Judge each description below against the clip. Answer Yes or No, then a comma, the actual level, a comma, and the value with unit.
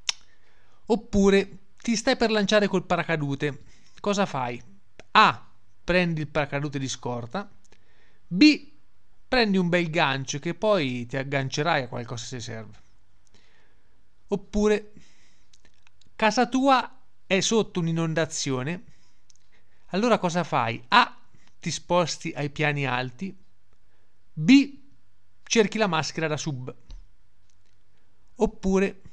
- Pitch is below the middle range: No, medium, 150 Hz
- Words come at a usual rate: No, slow, 105 wpm